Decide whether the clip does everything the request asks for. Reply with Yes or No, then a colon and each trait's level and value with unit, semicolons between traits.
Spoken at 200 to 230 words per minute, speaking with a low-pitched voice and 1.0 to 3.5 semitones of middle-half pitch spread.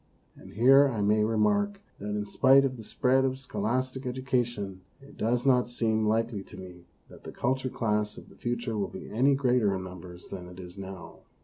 No: fast, 205 wpm; low, 115 Hz; average, 4.1 semitones